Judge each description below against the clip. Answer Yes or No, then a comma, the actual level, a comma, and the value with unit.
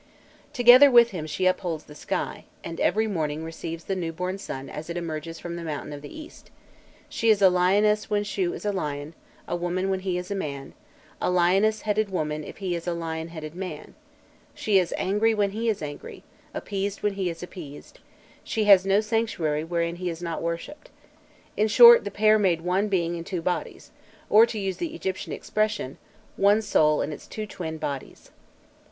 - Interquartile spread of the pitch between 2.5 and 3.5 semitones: No, average, 4.2 semitones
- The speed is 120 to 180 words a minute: No, average, 195 wpm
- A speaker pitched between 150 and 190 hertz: Yes, medium, 185 Hz